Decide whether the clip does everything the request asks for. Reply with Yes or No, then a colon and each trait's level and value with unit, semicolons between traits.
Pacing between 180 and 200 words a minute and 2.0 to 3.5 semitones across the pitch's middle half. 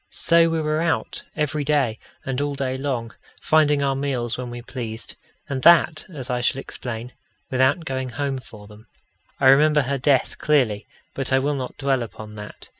Yes: average, 185 wpm; average, 3.1 semitones